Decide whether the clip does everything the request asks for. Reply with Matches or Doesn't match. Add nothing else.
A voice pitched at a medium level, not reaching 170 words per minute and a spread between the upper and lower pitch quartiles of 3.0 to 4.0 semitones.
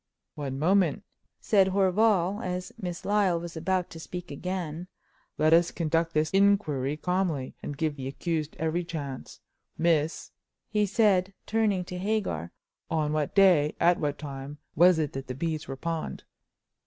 Matches